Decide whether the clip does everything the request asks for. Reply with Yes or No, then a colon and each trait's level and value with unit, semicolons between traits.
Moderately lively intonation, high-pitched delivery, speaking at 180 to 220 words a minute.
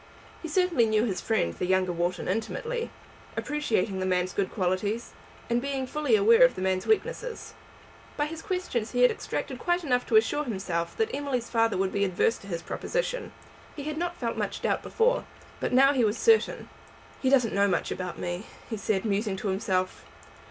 No: wide, 8.2 semitones; high, 230 Hz; average, 190 wpm